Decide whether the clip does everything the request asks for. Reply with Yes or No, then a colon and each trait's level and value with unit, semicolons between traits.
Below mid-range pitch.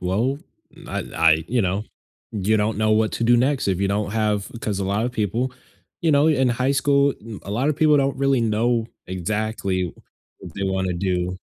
Yes: low, 110 Hz